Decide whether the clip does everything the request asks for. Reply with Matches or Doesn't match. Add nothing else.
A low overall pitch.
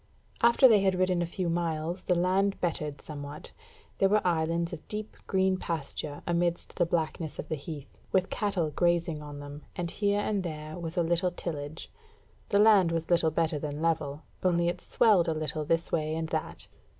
Doesn't match